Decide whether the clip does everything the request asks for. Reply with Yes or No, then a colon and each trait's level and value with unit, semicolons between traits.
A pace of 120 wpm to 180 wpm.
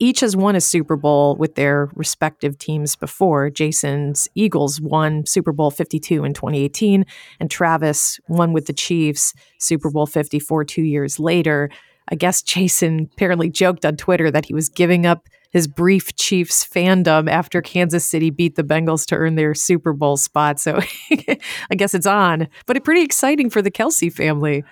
Yes: average, 175 wpm